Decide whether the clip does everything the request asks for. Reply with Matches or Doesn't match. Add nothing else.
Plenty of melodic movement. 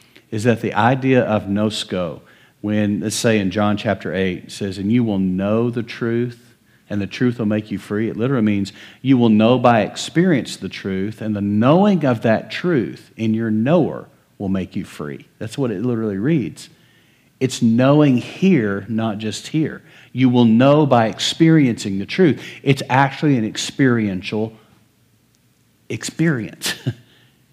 Doesn't match